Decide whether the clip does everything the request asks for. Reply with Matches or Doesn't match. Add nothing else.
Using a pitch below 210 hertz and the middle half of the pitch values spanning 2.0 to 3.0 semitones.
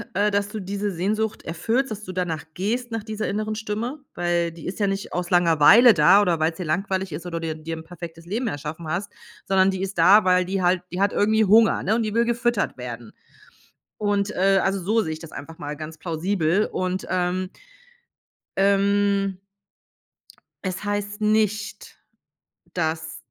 Doesn't match